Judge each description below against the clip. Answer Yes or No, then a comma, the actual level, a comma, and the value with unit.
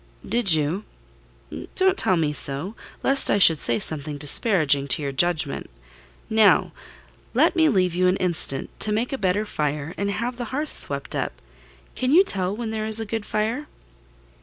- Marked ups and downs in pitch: Yes, wide, 6.4 semitones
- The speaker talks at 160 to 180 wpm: Yes, average, 170 wpm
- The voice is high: Yes, high, 195 Hz